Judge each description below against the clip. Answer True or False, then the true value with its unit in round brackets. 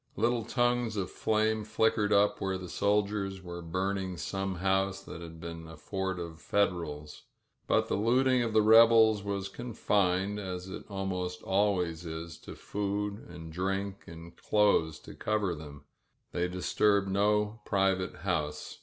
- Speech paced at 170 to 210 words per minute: False (150 wpm)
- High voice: False (95 Hz)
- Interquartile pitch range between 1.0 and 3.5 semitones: True (2.9 semitones)